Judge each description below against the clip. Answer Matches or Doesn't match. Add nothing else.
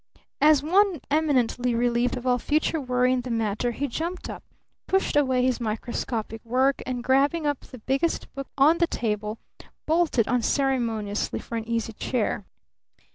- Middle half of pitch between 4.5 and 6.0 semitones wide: Doesn't match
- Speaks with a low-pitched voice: Doesn't match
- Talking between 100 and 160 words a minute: Matches